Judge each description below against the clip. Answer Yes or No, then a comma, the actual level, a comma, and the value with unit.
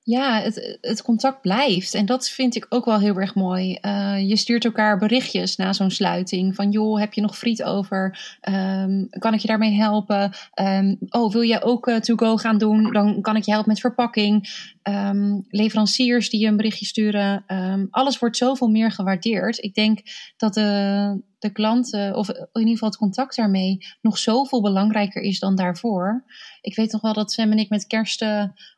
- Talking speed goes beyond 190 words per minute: Yes, fast, 200 wpm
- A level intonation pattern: Yes, narrow, 2.2 semitones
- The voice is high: Yes, high, 215 Hz